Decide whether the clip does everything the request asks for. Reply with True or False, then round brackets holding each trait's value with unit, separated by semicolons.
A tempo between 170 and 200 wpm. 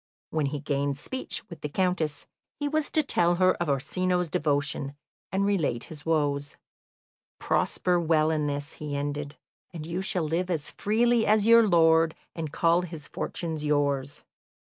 False (160 wpm)